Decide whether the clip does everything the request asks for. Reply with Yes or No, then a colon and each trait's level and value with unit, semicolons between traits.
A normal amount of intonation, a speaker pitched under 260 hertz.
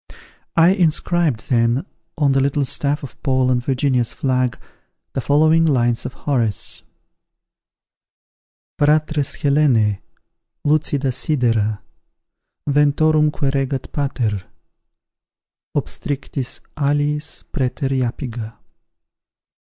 Yes: average, 3.1 semitones; medium, 140 Hz